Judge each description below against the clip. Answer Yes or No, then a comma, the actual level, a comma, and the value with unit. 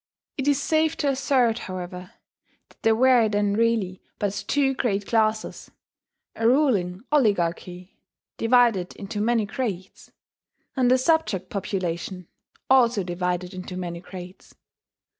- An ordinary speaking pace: No, slow, 120 wpm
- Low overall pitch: No, high, 210 Hz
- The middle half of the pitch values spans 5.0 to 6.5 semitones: Yes, wide, 5.5 semitones